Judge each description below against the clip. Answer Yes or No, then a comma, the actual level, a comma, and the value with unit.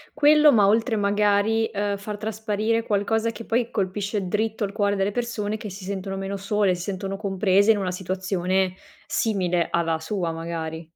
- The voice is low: No, high, 200 Hz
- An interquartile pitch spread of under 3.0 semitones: Yes, narrow, 2.4 semitones